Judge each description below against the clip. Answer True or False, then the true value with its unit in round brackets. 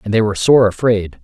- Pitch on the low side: True (110 Hz)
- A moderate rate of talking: False (245 wpm)